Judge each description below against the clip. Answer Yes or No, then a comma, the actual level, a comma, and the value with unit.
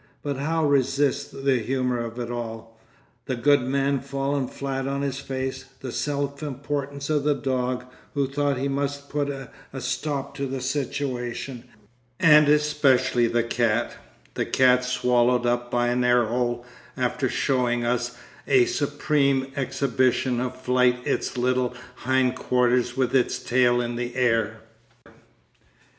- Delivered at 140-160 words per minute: Yes, average, 145 wpm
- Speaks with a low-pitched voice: Yes, low, 130 Hz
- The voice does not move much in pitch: Yes, narrow, 2.3 semitones